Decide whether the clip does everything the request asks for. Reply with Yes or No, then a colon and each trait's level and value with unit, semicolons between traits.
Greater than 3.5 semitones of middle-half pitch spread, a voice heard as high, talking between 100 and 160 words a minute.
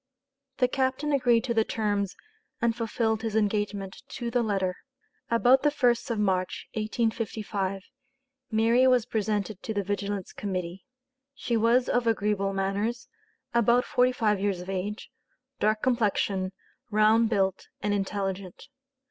No: average, 3.0 semitones; high, 215 Hz; slow, 135 wpm